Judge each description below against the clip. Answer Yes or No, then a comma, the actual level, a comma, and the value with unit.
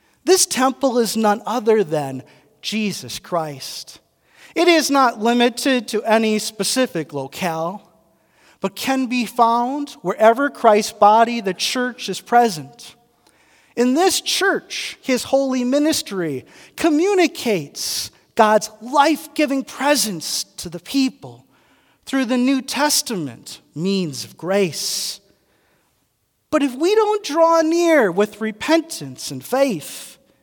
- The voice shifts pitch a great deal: Yes, wide, 6.6 semitones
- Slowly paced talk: Yes, slow, 115 wpm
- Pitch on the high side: Yes, high, 230 Hz